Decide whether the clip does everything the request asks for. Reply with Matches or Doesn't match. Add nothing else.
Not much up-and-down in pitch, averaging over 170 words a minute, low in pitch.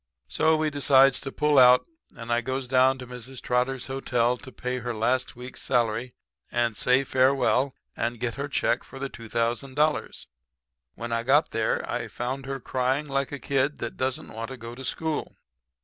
Matches